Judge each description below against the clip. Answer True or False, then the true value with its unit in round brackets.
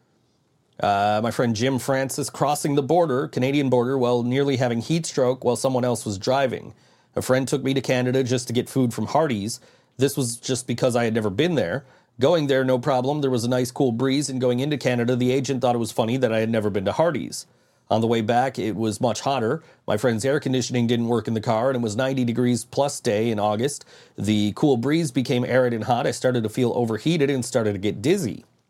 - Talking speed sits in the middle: False (230 wpm)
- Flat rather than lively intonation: True (2.3 semitones)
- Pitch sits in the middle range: False (125 Hz)